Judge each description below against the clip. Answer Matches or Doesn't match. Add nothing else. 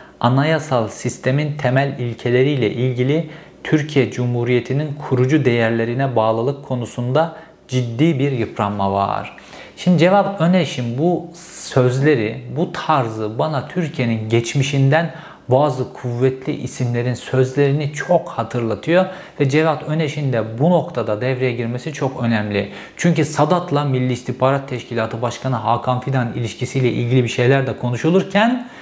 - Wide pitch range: Doesn't match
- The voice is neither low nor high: Doesn't match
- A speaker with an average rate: Matches